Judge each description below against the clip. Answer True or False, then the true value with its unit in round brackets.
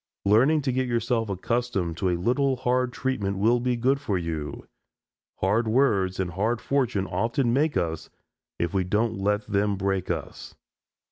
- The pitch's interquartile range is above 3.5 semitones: True (4.7 semitones)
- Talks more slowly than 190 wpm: True (160 wpm)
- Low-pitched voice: True (110 Hz)